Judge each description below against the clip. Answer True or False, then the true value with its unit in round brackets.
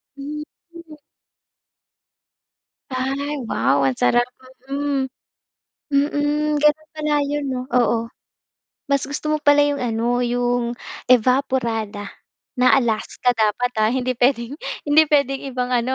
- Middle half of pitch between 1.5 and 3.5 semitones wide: True (3.2 semitones)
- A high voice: True (260 Hz)